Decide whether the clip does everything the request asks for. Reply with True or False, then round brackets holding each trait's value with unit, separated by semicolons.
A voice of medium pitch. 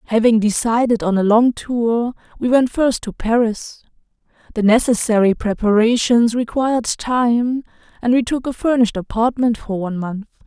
False (230 Hz)